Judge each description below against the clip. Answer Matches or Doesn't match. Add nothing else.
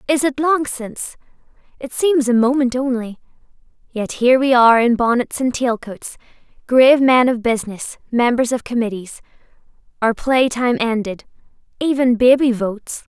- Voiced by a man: Doesn't match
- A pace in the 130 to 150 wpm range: Matches